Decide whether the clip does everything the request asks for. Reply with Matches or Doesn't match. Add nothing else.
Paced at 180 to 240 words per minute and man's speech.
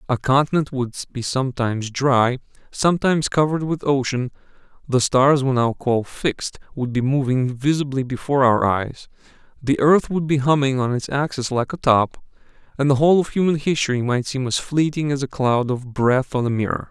Matches